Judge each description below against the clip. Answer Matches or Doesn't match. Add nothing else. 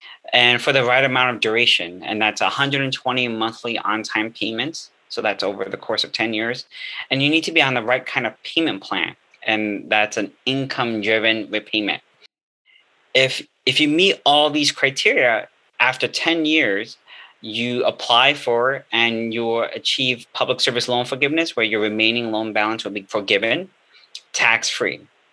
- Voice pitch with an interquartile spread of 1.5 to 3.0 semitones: Doesn't match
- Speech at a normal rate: Matches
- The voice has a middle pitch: Doesn't match